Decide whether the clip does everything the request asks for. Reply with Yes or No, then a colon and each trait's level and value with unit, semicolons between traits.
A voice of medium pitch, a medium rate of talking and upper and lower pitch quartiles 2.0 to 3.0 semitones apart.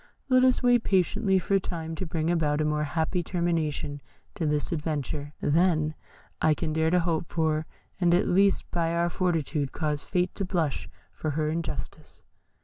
Yes: medium, 165 Hz; average, 170 wpm; average, 2.7 semitones